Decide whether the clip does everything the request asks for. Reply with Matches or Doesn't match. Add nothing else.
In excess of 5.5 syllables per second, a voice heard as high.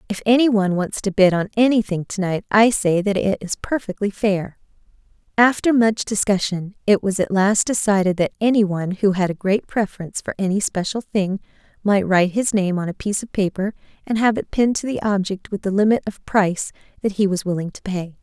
Matches